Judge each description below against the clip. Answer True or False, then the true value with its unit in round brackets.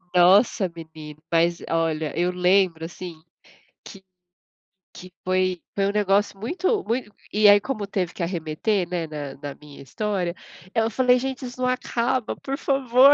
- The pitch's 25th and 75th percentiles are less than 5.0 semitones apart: False (5.6 semitones)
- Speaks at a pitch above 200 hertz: False (190 Hz)